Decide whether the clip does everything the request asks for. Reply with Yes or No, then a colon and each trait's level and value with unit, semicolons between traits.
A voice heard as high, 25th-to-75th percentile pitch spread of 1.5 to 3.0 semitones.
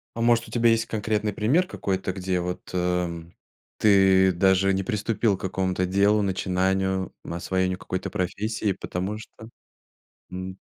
No: very low, 95 Hz; narrow, 2.4 semitones